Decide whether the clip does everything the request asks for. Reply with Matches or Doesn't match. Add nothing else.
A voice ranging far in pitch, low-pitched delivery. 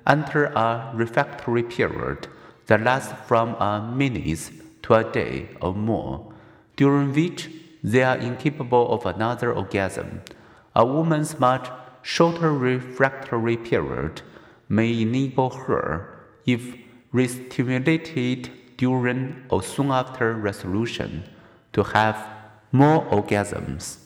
Doesn't match